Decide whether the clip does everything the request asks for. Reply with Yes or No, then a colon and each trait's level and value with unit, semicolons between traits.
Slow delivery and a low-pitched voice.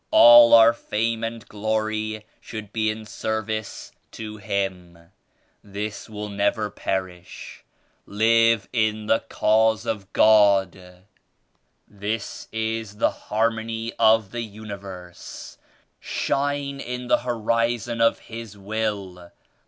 Yes: slow, 105 wpm; low, 110 Hz